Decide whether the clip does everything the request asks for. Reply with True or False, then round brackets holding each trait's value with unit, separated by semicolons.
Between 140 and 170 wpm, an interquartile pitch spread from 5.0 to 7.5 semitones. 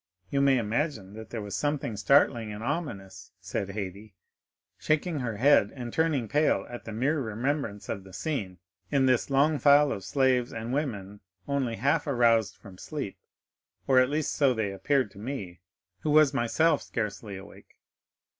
True (165 wpm; 5.4 semitones)